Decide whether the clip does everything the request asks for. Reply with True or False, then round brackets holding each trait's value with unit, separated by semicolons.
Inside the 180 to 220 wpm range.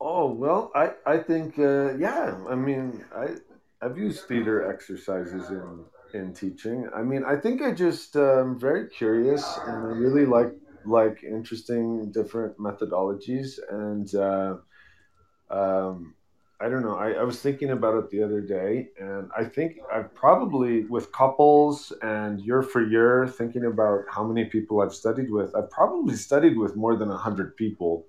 False (165 wpm)